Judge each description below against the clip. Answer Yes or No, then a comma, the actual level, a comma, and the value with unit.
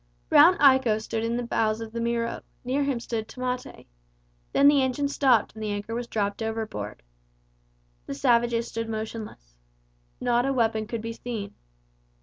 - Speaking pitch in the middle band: No, high, 230 Hz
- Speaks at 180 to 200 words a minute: No, average, 160 wpm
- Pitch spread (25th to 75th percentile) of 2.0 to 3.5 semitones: Yes, narrow, 2.4 semitones